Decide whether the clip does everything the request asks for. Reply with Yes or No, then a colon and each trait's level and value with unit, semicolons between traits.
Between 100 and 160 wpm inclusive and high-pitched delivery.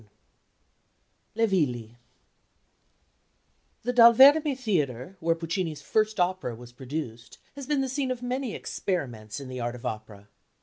No: average, 140 wpm; medium, 170 Hz